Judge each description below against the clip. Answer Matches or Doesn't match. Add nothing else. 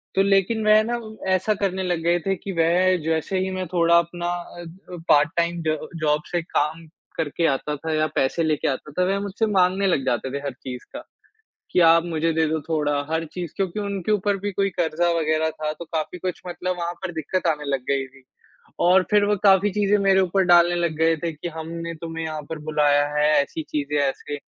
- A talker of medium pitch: Matches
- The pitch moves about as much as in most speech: Matches